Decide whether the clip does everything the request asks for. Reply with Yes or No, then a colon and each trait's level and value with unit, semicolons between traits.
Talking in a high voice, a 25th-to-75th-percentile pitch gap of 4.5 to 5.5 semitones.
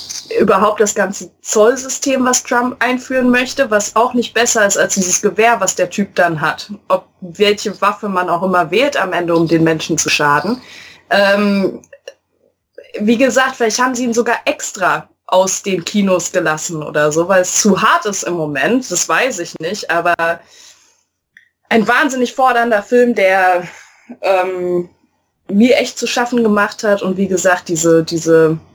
Yes: high, 200 Hz; average, 5.1 semitones